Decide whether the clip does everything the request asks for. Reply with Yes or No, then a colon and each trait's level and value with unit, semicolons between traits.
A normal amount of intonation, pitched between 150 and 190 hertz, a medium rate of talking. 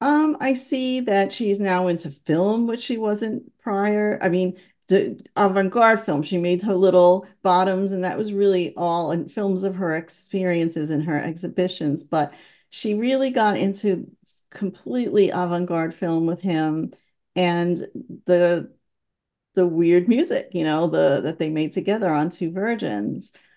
Yes: average, 3.4 semitones; medium, 185 Hz; average, 155 wpm